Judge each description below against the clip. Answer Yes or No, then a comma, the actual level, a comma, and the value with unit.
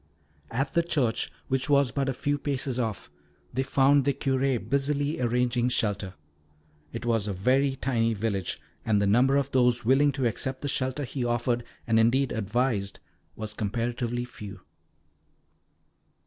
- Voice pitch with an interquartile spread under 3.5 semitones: Yes, average, 3.1 semitones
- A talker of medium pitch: No, low, 125 Hz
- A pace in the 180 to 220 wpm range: No, average, 150 wpm